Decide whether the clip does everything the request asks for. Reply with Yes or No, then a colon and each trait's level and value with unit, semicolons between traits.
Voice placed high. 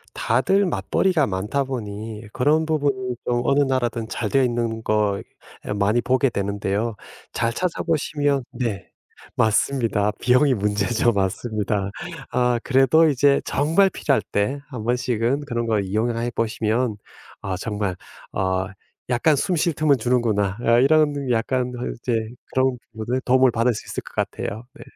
No: low, 120 Hz